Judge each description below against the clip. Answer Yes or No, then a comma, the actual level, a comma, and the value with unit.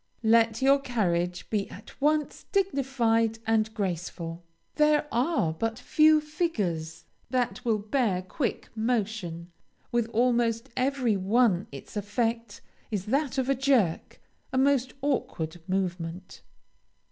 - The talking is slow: Yes, slow, 120 wpm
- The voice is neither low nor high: No, high, 225 Hz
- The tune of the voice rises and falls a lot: Yes, wide, 5.8 semitones